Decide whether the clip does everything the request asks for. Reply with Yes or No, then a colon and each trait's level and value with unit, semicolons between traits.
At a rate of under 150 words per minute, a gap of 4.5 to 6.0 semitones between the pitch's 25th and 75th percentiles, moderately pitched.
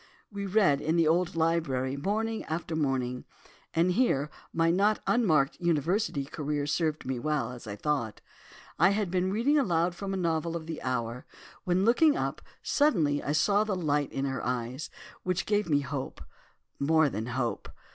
No: average, 170 wpm; average, 5.2 semitones; medium, 160 Hz